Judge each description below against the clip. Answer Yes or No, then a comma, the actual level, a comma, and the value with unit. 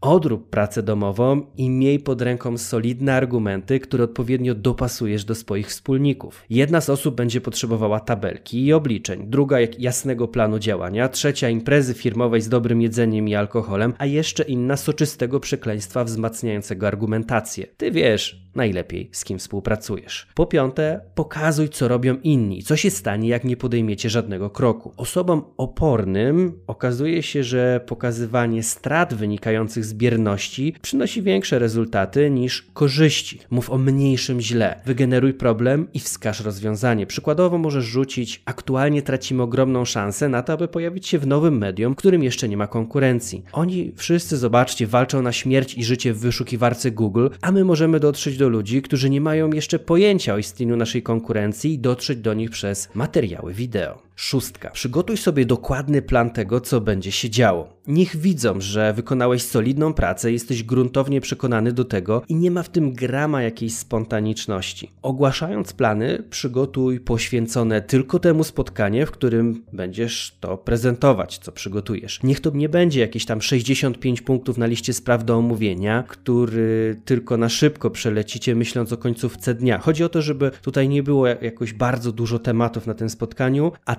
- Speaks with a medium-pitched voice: No, low, 125 Hz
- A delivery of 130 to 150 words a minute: No, fast, 160 wpm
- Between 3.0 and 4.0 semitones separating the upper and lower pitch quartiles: Yes, average, 3.6 semitones